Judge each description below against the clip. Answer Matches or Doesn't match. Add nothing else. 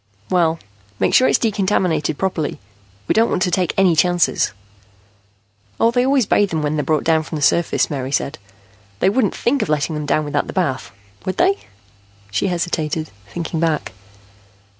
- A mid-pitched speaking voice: Matches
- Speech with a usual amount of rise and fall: Matches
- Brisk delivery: Doesn't match